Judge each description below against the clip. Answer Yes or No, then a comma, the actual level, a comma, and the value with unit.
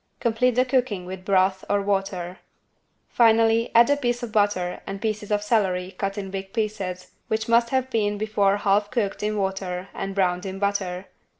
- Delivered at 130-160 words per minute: No, average, 180 wpm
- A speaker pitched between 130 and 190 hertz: No, high, 205 Hz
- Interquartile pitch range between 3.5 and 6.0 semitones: No, average, 2.7 semitones